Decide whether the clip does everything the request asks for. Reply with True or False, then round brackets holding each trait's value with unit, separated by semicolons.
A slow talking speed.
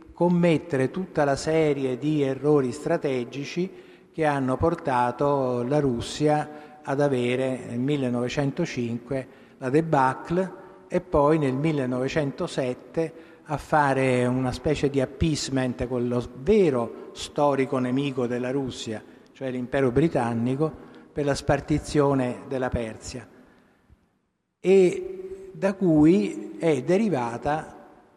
True (100 wpm)